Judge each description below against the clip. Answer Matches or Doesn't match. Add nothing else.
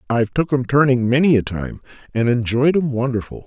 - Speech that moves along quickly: Doesn't match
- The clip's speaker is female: Doesn't match